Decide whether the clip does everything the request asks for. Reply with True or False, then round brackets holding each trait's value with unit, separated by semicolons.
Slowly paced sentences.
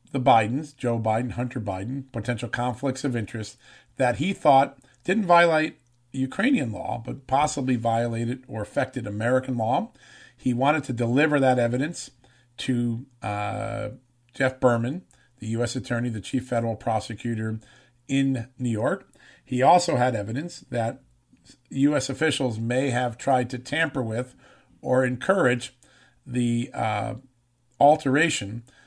True (130 wpm)